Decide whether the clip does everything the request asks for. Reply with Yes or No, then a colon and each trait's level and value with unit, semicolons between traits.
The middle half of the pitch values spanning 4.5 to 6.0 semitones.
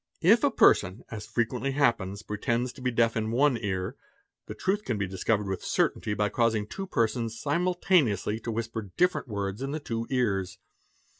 No: average, 3.7 semitones